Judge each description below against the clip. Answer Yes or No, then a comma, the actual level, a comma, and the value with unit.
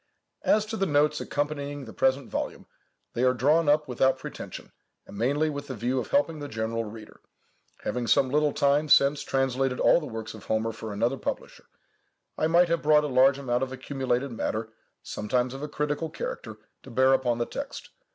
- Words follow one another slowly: No, average, 190 wpm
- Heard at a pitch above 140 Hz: No, low, 135 Hz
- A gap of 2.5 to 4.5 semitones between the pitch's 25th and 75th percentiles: Yes, average, 3.4 semitones